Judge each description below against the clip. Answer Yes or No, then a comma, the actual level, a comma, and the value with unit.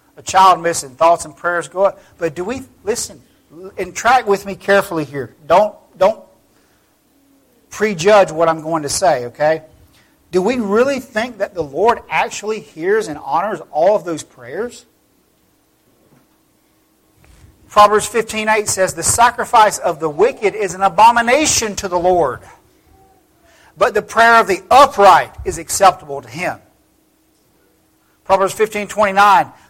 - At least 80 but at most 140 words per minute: Yes, slow, 135 wpm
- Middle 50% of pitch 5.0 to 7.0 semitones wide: Yes, wide, 5.4 semitones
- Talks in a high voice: Yes, high, 200 Hz